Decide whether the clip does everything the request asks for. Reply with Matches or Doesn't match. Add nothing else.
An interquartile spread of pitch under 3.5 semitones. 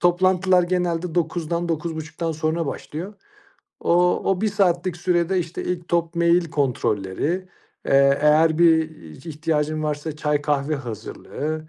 Matches